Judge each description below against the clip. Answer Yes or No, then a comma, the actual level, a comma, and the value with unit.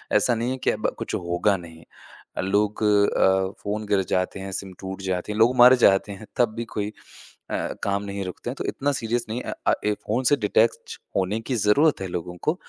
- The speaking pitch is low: Yes, low, 105 Hz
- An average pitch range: Yes, average, 3.2 semitones